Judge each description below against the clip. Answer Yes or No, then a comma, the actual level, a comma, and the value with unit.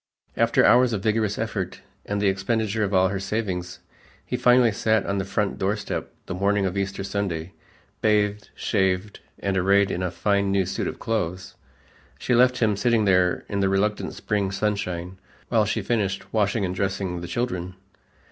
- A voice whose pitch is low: Yes, low, 100 Hz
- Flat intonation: Yes, narrow, 2.1 semitones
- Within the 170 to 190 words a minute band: Yes, average, 175 wpm